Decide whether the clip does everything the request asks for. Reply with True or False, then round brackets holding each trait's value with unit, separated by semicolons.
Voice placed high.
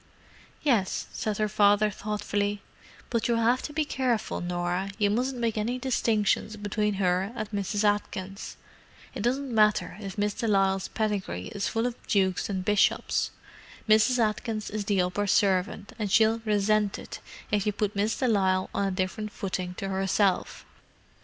True (205 Hz)